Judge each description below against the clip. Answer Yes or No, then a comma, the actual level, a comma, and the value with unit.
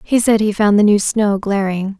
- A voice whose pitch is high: Yes, high, 205 Hz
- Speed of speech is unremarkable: No, fast, 240 wpm